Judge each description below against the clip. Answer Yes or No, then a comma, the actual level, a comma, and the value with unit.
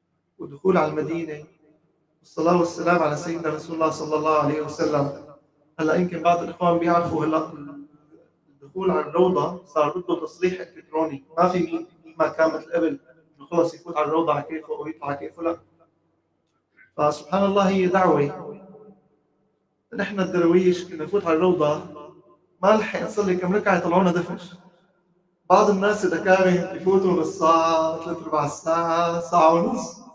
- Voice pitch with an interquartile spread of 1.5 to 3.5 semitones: Yes, average, 2.8 semitones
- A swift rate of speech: Yes, fast, 140 wpm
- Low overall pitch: No, medium, 165 Hz